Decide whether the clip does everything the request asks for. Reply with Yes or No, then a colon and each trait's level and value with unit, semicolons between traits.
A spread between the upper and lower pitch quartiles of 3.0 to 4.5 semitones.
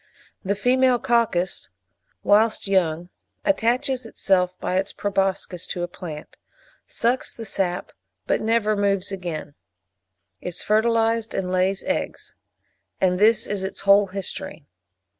Yes: average, 3.7 semitones